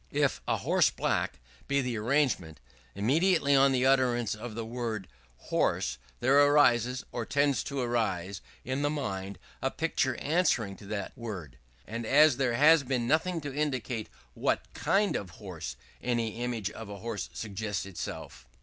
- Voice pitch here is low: Yes, low, 120 Hz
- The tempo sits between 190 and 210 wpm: No, average, 160 wpm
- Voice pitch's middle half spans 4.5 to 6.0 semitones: Yes, average, 4.8 semitones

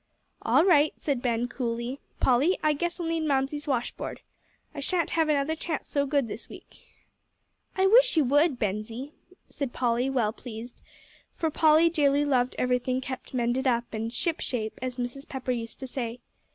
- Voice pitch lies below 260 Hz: No, very high, 265 Hz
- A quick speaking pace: No, average, 165 wpm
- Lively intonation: No, average, 3.9 semitones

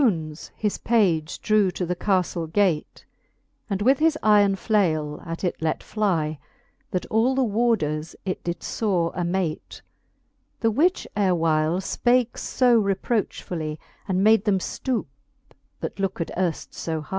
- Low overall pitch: No, high, 190 Hz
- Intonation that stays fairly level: No, average, 4.7 semitones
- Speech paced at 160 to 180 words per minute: No, average, 140 wpm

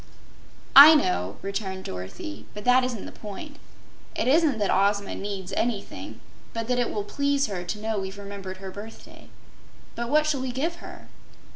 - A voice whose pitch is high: Yes, high, 210 Hz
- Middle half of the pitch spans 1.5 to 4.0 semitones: No, average, 5.0 semitones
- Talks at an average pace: Yes, average, 170 wpm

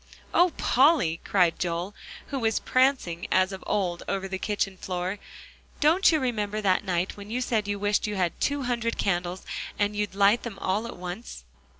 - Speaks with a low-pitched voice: No, high, 205 Hz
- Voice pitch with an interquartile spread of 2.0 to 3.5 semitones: No, average, 4.0 semitones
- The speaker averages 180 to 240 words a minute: Yes, average, 185 wpm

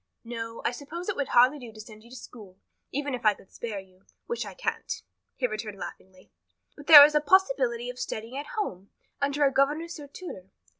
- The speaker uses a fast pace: Yes, fast, 210 wpm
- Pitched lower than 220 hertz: No, very high, 250 Hz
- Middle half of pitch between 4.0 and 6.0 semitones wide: Yes, average, 5.2 semitones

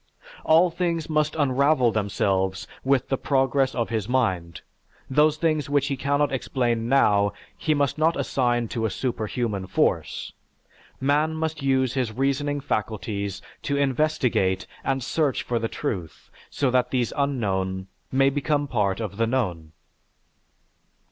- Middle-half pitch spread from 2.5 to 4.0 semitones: No, average, 4.8 semitones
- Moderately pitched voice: No, low, 130 Hz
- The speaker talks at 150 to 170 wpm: No, average, 140 wpm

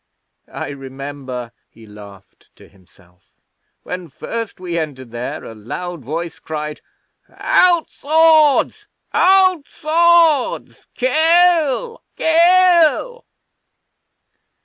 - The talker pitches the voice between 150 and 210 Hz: Yes, medium, 185 Hz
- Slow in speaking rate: Yes, slow, 85 wpm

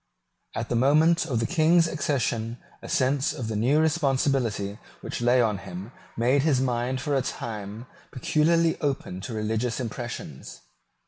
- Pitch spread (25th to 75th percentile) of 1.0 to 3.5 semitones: No, average, 4.5 semitones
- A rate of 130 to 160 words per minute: Yes, average, 150 wpm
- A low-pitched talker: Yes, low, 125 Hz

